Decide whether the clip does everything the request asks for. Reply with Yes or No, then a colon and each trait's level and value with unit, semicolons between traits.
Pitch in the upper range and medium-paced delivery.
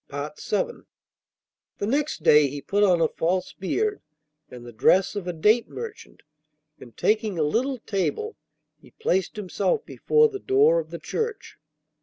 Yes: high, 215 Hz; average, 155 wpm